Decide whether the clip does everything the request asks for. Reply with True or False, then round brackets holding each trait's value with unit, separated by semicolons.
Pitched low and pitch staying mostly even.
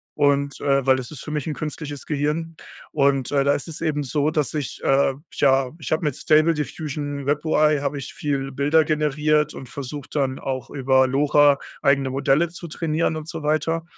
False (145 Hz; 1.9 semitones)